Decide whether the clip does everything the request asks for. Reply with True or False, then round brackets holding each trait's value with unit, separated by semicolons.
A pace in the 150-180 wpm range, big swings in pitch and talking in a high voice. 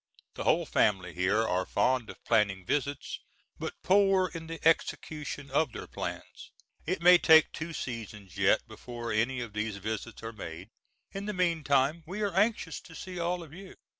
False (175 wpm; 7.8 semitones; 140 Hz)